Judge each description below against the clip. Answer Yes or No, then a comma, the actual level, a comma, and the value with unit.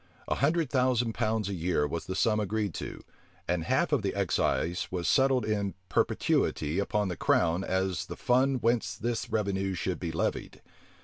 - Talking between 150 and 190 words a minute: Yes, average, 175 wpm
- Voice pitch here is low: Yes, low, 100 Hz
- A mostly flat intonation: No, average, 4.7 semitones